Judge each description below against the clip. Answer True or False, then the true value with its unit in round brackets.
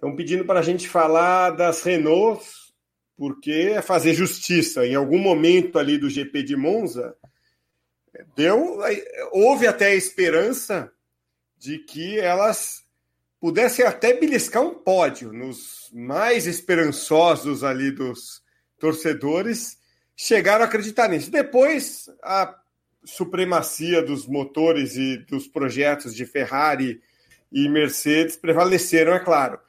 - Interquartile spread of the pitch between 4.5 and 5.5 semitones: True (5.0 semitones)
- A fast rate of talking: False (115 wpm)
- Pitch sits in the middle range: True (165 Hz)